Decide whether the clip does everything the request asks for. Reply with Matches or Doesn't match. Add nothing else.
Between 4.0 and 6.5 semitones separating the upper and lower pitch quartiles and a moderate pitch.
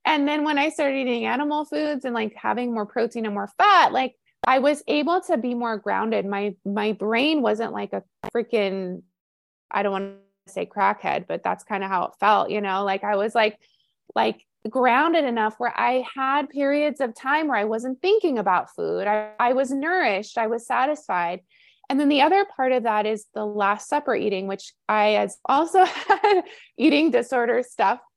Doesn't match